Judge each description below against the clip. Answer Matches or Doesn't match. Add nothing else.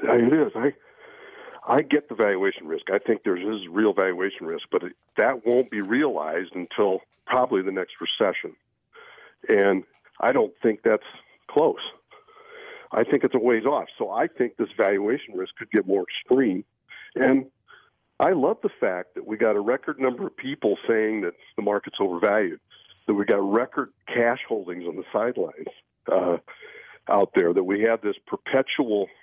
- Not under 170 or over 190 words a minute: Matches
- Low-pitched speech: Doesn't match